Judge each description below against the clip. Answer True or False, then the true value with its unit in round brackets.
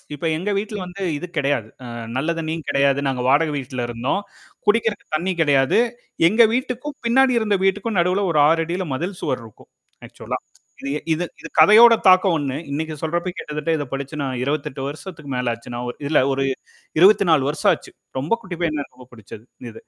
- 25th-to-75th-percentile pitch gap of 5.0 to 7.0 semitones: True (5.6 semitones)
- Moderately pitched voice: True (160 Hz)